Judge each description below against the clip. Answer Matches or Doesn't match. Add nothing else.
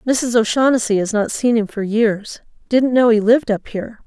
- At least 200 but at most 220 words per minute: Doesn't match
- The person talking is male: Doesn't match